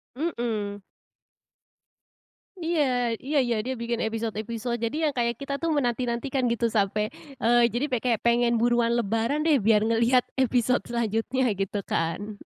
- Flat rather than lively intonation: Yes, narrow, 2.2 semitones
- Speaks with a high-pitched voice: Yes, high, 235 Hz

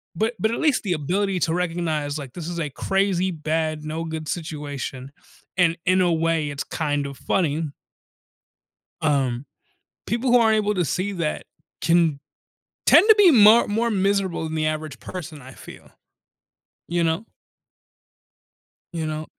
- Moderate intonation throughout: Yes, average, 4.1 semitones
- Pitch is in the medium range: Yes, medium, 165 Hz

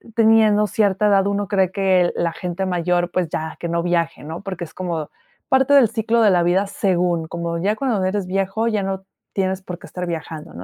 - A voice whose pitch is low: No, medium, 185 Hz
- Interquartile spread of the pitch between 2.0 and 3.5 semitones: Yes, average, 2.9 semitones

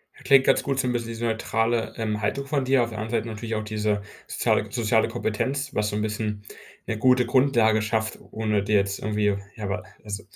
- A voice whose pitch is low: Yes, low, 110 Hz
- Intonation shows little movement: Yes, narrow, 2.2 semitones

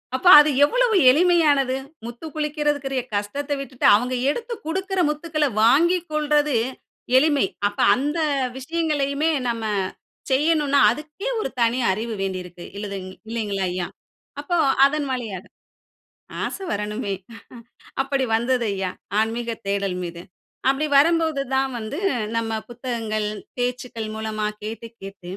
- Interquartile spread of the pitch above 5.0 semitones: Yes, wide, 5.5 semitones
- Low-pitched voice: No, very high, 260 Hz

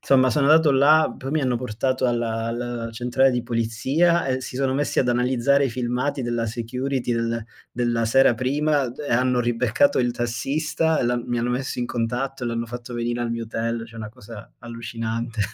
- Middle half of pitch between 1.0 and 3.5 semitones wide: Yes, narrow, 2.4 semitones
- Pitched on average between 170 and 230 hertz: No, low, 120 Hz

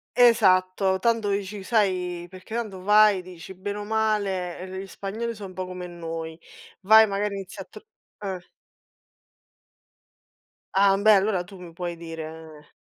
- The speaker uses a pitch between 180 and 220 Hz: Yes, high, 190 Hz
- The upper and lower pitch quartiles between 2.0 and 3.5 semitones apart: Yes, narrow, 2.6 semitones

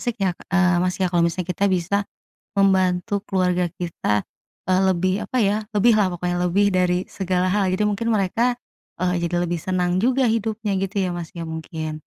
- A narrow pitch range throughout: Yes, narrow, 2.1 semitones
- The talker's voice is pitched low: No, medium, 185 Hz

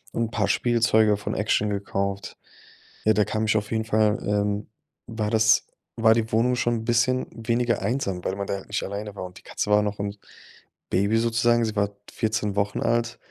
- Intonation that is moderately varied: No, narrow, 2.1 semitones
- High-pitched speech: No, low, 110 Hz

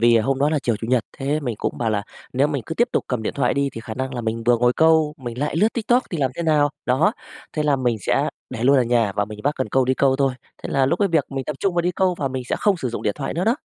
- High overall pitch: No, low, 135 Hz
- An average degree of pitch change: Yes, average, 4.2 semitones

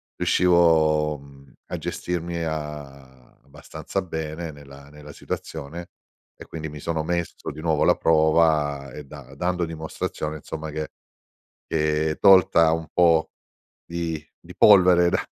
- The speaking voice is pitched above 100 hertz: No, very low, 80 Hz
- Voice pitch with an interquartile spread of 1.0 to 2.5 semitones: Yes, narrow, 2.2 semitones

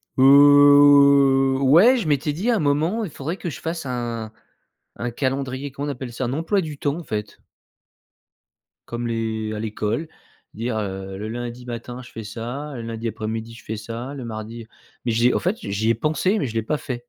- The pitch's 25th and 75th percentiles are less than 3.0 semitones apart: No, average, 4.1 semitones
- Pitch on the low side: Yes, low, 125 Hz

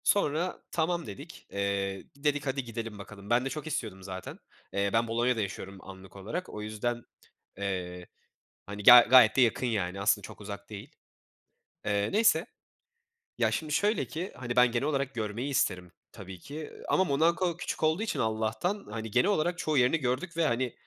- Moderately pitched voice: No, low, 120 Hz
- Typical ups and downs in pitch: No, wide, 7.0 semitones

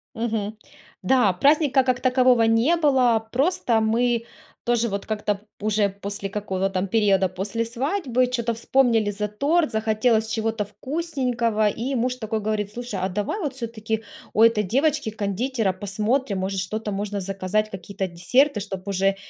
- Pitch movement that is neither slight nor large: Yes, average, 3.7 semitones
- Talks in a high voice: Yes, high, 220 Hz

